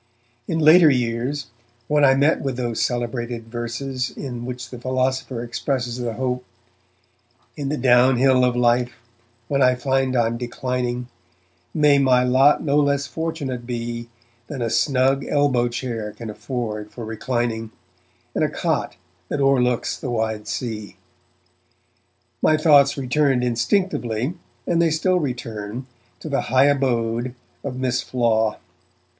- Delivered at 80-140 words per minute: Yes, slow, 135 wpm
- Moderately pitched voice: No, low, 125 Hz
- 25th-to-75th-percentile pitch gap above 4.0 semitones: No, narrow, 2.6 semitones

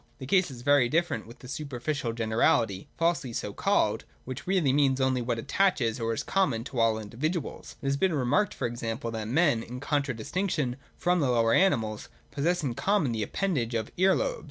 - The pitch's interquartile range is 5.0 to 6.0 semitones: Yes, wide, 5.6 semitones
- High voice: No, low, 130 Hz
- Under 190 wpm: No, average, 195 wpm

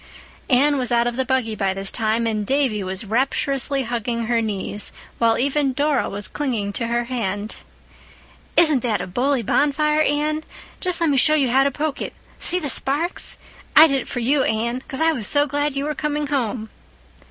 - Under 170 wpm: No, average, 195 wpm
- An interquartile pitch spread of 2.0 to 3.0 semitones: No, average, 4.2 semitones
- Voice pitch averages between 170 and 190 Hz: No, very high, 260 Hz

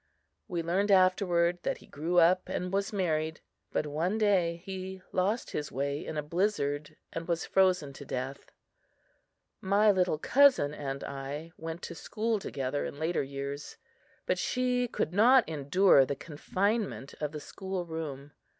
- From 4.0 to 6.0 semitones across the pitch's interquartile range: Yes, average, 4.7 semitones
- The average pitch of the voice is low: No, medium, 170 Hz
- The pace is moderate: Yes, average, 155 wpm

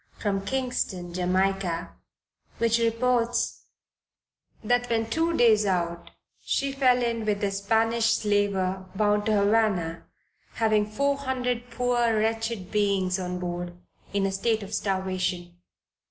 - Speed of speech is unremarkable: No, slow, 125 wpm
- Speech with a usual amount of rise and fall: Yes, average, 3.6 semitones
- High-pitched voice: Yes, high, 210 Hz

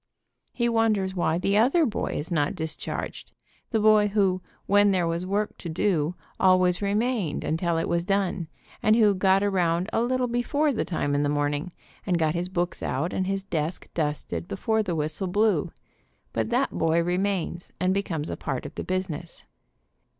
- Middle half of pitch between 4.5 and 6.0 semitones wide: No, average, 3.8 semitones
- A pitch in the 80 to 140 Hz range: No, medium, 185 Hz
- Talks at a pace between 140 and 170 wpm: No, average, 180 wpm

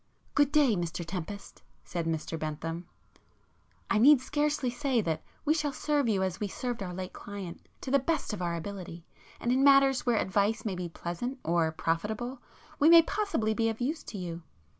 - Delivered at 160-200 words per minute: Yes, average, 180 wpm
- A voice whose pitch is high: Yes, high, 210 Hz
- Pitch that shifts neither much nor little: No, wide, 7.6 semitones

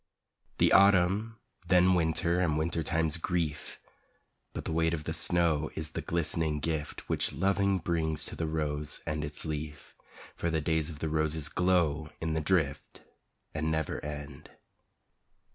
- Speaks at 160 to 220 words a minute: No, average, 150 wpm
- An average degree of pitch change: No, narrow, 2.0 semitones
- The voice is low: Yes, very low, 80 Hz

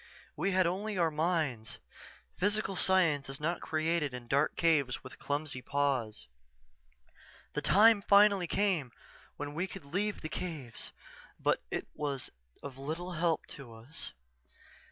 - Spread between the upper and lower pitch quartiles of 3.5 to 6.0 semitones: Yes, average, 4.8 semitones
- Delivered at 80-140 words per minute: Yes, slow, 135 wpm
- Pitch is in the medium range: Yes, medium, 155 Hz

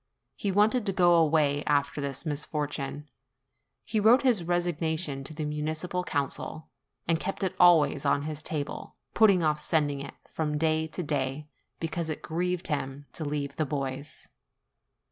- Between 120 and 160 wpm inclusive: Yes, average, 155 wpm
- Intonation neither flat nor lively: Yes, average, 3.2 semitones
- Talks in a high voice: No, medium, 155 Hz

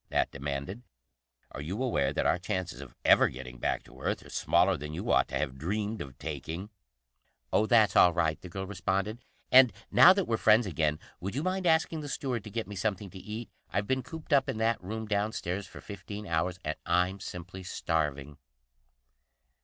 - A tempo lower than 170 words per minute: No, average, 195 wpm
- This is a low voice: Yes, very low, 95 Hz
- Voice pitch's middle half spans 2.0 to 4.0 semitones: No, average, 5.1 semitones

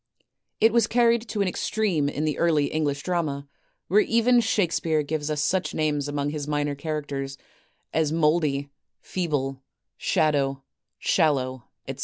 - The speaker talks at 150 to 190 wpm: No, average, 140 wpm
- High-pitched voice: No, medium, 155 Hz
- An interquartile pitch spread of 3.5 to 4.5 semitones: Yes, average, 3.8 semitones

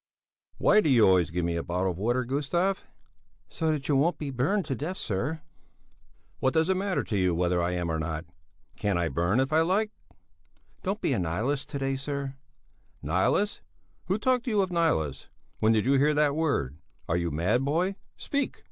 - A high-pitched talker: No, low, 135 Hz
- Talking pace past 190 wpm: Yes, average, 200 wpm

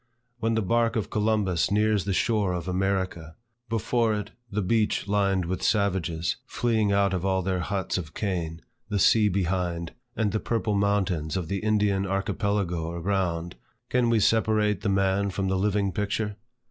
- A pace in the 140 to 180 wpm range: Yes, average, 165 wpm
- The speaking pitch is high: No, low, 100 Hz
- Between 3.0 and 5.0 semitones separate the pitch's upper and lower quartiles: No, narrow, 2.4 semitones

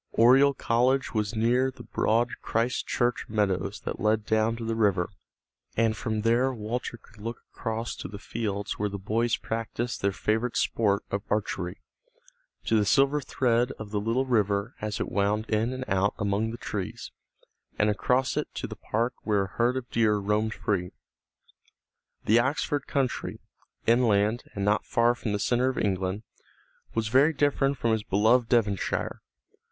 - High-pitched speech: No, low, 110 Hz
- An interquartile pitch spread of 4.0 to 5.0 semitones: No, average, 2.7 semitones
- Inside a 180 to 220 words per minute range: No, average, 170 wpm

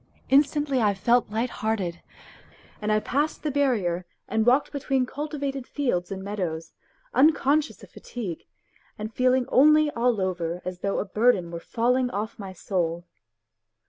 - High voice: Yes, high, 225 Hz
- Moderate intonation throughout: No, wide, 6.2 semitones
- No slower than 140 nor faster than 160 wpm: Yes, average, 145 wpm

